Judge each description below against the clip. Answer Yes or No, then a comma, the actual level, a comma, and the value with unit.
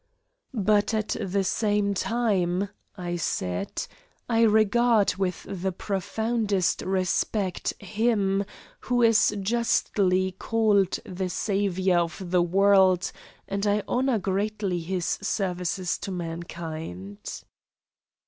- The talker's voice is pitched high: Yes, high, 195 Hz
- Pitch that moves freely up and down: No, average, 2.8 semitones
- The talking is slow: Yes, slow, 100 wpm